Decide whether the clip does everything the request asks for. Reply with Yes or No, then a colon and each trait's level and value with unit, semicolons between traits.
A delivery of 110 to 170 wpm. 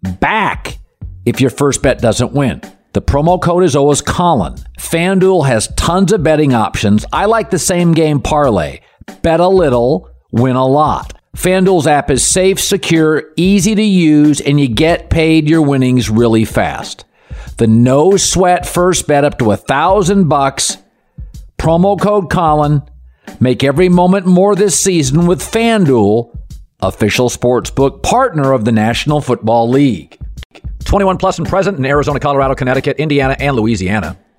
Yes: average, 155 wpm